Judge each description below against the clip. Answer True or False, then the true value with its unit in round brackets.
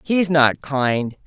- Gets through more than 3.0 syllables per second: False (2.7 syllables/s)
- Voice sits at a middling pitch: True (145 Hz)